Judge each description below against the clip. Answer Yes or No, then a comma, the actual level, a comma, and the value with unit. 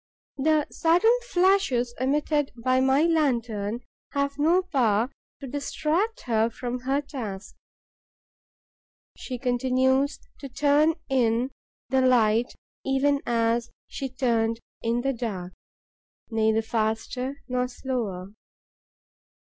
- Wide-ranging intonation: No, average, 3.6 semitones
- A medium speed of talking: No, slow, 105 wpm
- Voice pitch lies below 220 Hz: No, very high, 255 Hz